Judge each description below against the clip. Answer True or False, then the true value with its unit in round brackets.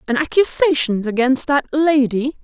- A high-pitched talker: True (270 Hz)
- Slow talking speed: True (125 wpm)